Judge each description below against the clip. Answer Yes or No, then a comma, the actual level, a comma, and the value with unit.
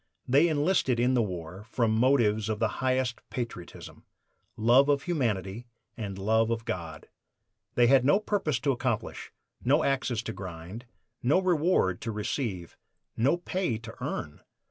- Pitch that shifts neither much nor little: Yes, average, 4.6 semitones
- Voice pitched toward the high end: No, low, 120 Hz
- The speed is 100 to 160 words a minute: Yes, average, 145 wpm